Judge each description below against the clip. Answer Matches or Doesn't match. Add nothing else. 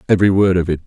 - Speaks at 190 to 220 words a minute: Doesn't match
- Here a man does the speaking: Matches